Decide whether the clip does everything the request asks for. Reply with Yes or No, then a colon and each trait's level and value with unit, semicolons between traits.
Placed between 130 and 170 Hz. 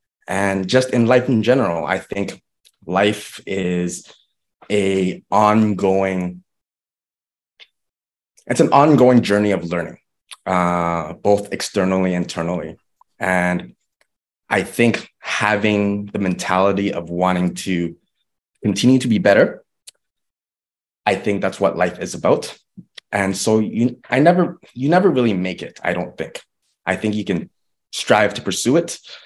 No: low, 100 Hz